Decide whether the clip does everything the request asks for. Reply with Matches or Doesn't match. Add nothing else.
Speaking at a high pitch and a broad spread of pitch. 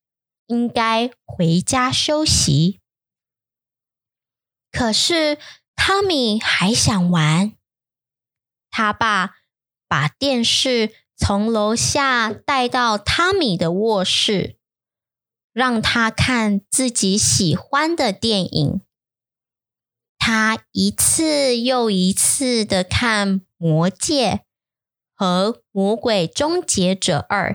Matches